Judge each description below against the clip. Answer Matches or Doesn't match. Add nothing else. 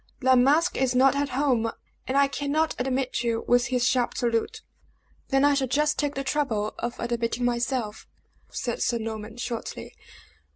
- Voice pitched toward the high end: Matches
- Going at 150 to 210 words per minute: Matches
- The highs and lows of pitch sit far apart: Doesn't match